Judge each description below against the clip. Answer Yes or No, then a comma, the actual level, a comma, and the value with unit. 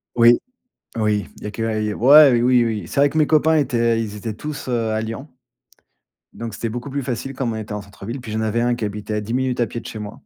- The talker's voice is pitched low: Yes, low, 115 Hz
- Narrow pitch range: No, average, 3.0 semitones